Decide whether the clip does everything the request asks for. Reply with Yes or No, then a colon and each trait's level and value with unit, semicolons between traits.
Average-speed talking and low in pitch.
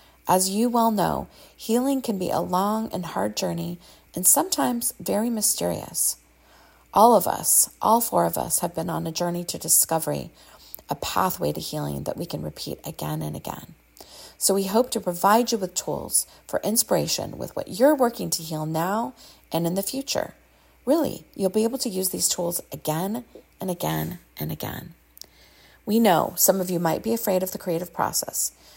No: average, 180 wpm; medium, 185 Hz